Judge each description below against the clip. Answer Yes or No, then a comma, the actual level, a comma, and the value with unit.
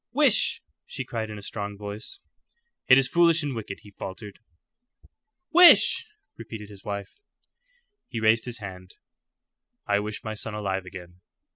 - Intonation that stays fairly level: Yes, narrow, 2.3 semitones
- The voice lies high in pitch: No, low, 105 Hz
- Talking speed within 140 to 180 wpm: Yes, average, 145 wpm